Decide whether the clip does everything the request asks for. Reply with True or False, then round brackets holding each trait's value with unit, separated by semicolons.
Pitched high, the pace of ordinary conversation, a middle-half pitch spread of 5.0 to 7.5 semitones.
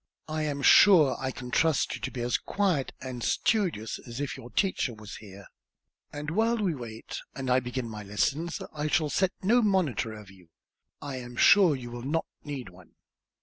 False (135 Hz; 190 wpm; 5.5 semitones)